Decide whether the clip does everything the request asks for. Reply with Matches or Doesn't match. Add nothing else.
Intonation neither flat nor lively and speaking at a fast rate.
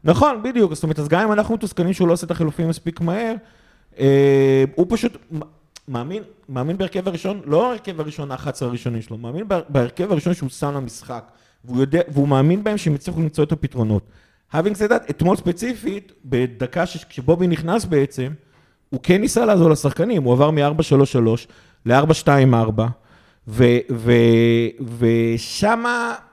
Doesn't match